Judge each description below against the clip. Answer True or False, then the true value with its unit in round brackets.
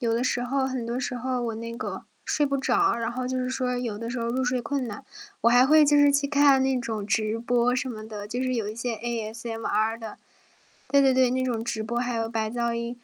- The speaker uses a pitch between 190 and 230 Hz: False (240 Hz)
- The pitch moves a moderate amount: False (2.2 semitones)